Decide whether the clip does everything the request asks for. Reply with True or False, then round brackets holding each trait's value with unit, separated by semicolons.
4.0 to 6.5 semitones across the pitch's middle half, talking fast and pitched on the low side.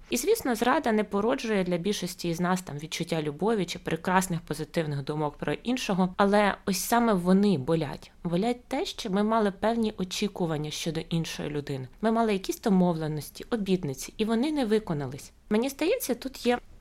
False (5.4 semitones; 165 wpm; 190 Hz)